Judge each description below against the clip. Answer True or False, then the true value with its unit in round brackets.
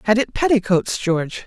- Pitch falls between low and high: False (210 Hz)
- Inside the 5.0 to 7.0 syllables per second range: True (5.4 syllables/s)